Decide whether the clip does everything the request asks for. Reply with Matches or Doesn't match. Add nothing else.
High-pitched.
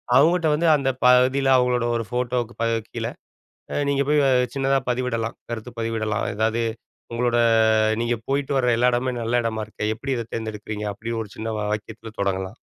Doesn't match